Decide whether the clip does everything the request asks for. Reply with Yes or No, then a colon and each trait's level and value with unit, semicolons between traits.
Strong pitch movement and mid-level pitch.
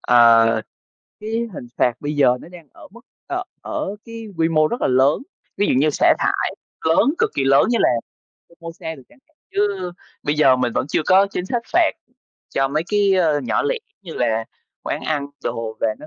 Yes: wide, 7.0 semitones; medium, 155 Hz